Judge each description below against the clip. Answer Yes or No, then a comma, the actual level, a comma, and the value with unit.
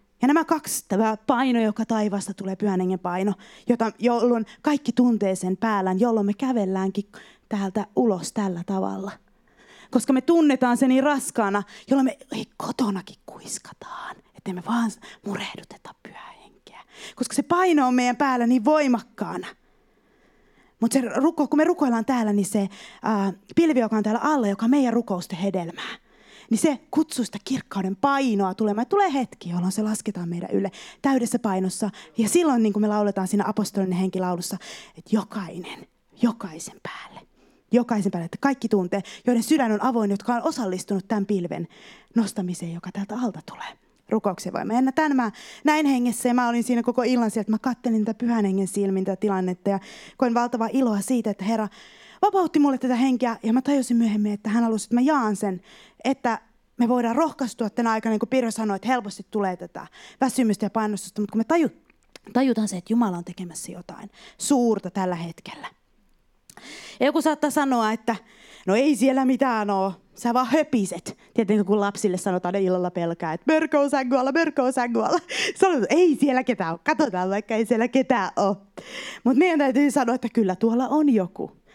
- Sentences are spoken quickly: Yes, fast, 175 wpm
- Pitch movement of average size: Yes, average, 4.4 semitones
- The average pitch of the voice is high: Yes, high, 225 Hz